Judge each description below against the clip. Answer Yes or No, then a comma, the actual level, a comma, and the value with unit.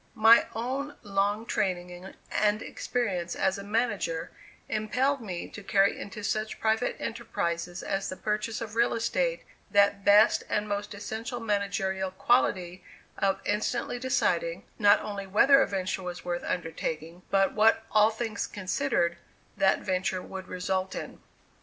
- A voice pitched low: No, high, 205 Hz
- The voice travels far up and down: No, average, 3.0 semitones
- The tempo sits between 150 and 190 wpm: No, average, 140 wpm